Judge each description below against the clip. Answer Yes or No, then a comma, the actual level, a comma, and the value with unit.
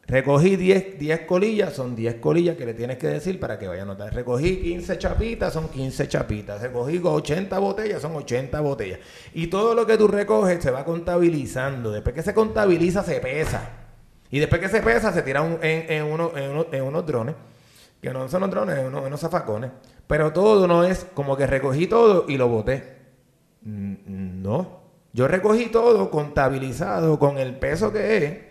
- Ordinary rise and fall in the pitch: No, wide, 5.8 semitones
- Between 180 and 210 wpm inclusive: Yes, average, 185 wpm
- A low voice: No, medium, 155 Hz